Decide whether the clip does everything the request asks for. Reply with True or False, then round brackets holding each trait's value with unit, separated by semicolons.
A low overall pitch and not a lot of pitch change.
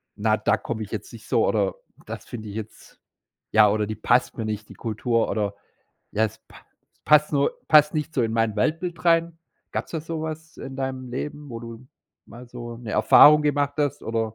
False (125 Hz; 5.2 semitones)